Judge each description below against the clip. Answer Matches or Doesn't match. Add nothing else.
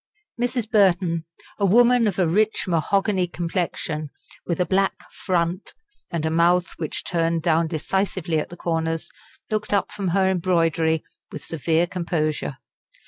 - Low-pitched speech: Doesn't match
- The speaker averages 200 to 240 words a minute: Doesn't match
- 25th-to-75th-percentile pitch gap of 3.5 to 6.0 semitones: Doesn't match